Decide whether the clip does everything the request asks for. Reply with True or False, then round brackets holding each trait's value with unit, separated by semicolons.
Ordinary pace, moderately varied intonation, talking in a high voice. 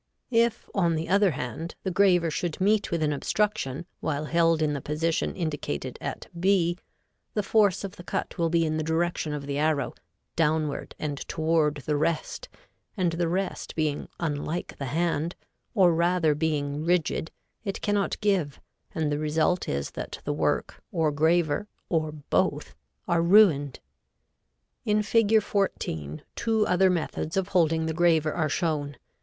False (160 wpm; 3.2 semitones; 165 Hz)